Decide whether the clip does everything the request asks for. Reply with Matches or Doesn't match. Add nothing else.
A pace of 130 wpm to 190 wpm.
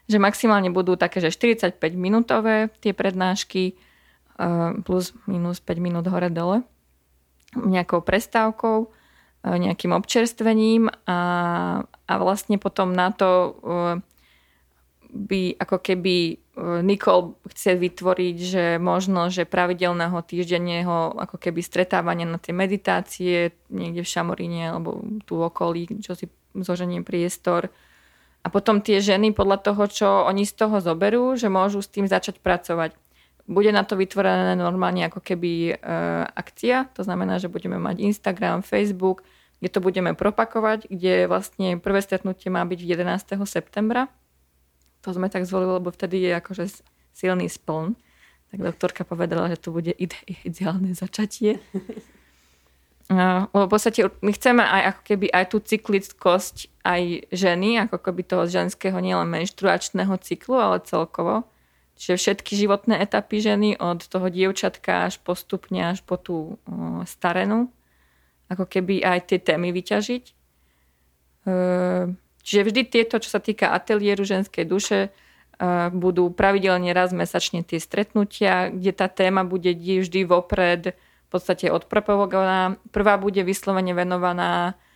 Matches